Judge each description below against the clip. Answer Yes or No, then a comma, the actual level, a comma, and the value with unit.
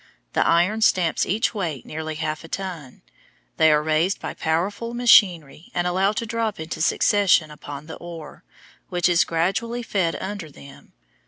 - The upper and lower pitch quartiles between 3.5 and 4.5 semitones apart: Yes, average, 4.2 semitones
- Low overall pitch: No, medium, 175 Hz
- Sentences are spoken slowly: No, average, 160 wpm